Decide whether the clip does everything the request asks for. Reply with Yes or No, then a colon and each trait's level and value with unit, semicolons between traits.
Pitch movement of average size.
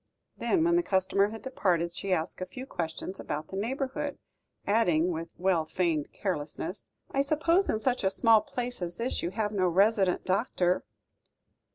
No: wide, 5.8 semitones